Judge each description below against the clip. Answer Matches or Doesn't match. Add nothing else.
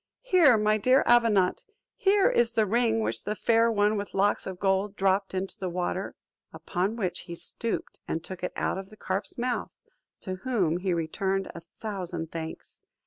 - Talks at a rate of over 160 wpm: Matches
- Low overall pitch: Doesn't match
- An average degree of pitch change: Matches